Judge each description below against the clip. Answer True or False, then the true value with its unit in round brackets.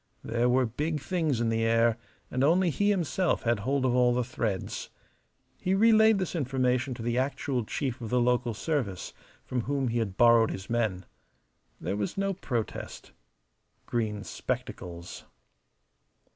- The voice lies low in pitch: True (125 Hz)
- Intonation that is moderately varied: True (4.0 semitones)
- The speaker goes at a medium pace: True (155 wpm)